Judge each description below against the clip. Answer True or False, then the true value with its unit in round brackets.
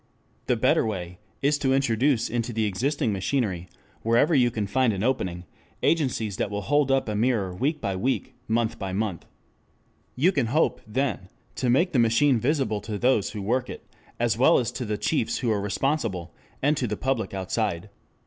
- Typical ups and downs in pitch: True (4.5 semitones)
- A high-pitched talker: False (115 Hz)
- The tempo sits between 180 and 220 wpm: True (185 wpm)